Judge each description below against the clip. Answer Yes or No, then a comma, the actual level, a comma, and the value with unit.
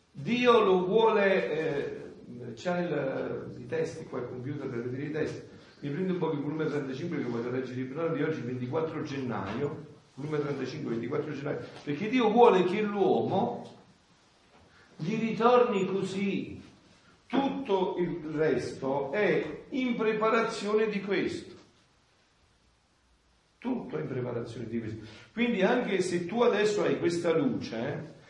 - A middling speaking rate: Yes, average, 135 wpm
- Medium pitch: Yes, medium, 165 Hz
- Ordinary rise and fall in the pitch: No, wide, 6.8 semitones